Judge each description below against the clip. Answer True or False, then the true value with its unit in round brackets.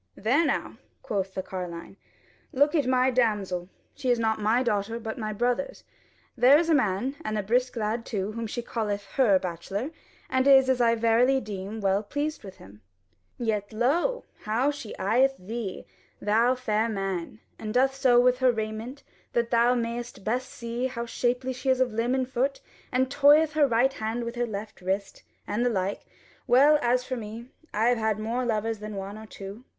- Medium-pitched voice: False (235 Hz)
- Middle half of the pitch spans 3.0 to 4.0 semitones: True (3.4 semitones)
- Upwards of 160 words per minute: True (190 wpm)